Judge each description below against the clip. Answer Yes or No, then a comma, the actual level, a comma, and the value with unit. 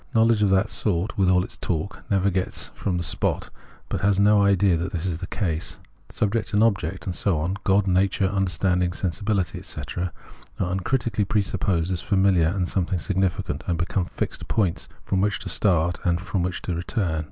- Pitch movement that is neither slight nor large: No, narrow, 2.3 semitones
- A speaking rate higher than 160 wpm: Yes, average, 185 wpm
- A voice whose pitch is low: Yes, very low, 95 Hz